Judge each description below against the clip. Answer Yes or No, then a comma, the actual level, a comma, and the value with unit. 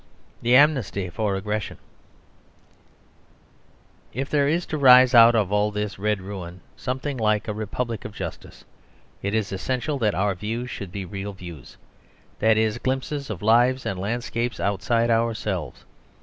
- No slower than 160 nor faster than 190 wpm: No, average, 150 wpm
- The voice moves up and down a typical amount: Yes, average, 3.9 semitones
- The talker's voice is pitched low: Yes, low, 110 Hz